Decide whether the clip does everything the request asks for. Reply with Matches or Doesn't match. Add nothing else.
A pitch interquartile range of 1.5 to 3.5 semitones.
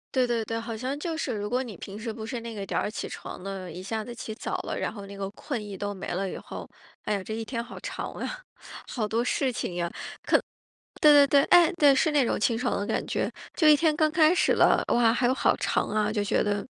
Doesn't match